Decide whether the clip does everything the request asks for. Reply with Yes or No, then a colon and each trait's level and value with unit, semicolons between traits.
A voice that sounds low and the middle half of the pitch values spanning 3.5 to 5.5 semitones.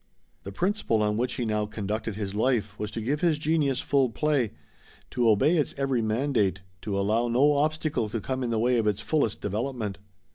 Yes: low, 115 Hz; average, 4.7 semitones